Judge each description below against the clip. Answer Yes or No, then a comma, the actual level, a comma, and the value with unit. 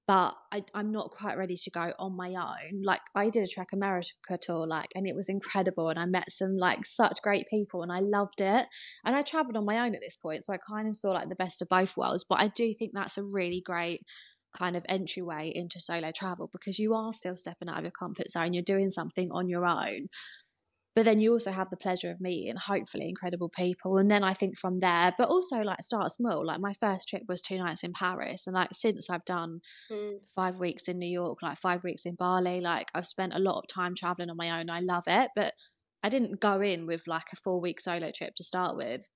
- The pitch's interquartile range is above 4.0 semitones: No, narrow, 2.4 semitones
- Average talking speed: No, fast, 245 wpm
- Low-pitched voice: No, medium, 185 Hz